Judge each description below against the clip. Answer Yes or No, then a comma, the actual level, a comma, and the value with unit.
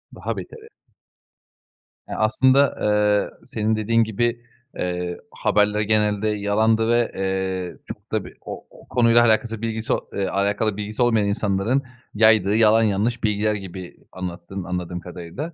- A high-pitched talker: No, low, 105 Hz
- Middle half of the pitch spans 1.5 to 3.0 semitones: Yes, narrow, 2.6 semitones